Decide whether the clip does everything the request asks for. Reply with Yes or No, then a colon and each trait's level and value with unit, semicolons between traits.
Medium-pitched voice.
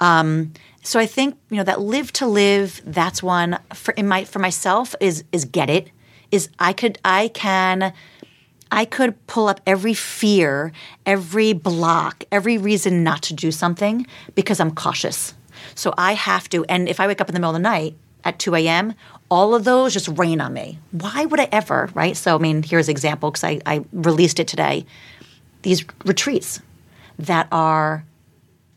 Yes: medium, 180 Hz